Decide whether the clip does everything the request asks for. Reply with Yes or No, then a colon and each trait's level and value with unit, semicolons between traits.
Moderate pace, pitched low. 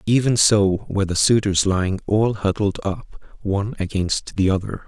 Yes: average, 160 wpm; low, 100 Hz